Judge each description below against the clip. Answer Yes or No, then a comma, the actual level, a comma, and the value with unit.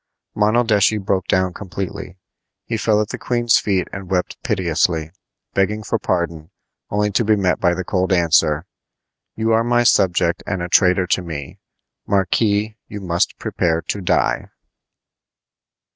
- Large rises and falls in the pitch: No, average, 3.3 semitones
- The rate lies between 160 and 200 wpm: No, average, 145 wpm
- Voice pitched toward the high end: No, very low, 95 Hz